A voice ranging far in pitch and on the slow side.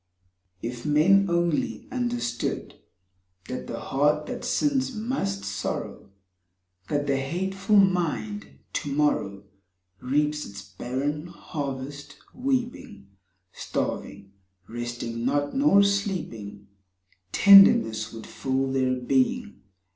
Yes: wide, 8.5 semitones; slow, 95 wpm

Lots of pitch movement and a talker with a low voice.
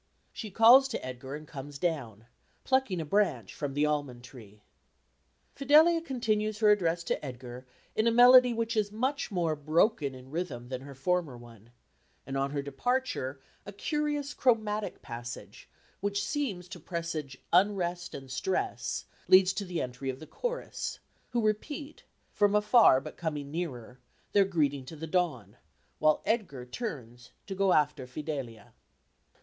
No: wide, 8.0 semitones; medium, 170 Hz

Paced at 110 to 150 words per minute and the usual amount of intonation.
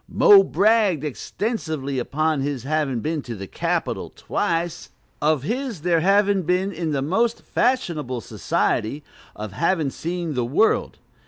No: average, 140 wpm; wide, 5.8 semitones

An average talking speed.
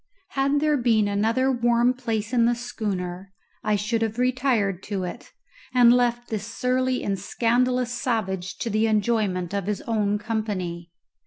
Yes: average, 155 wpm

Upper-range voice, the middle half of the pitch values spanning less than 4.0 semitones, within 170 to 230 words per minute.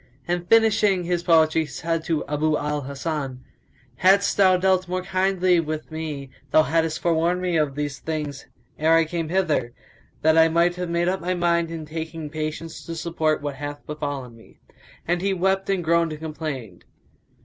No: medium, 165 Hz; average, 2.7 semitones; average, 180 wpm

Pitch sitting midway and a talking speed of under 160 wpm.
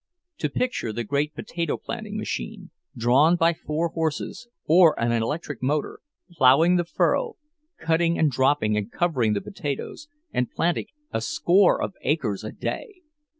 Yes: medium, 150 Hz; average, 150 wpm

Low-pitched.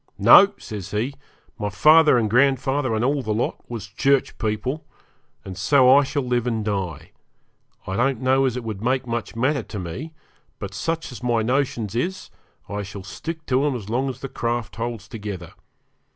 Yes: low, 120 Hz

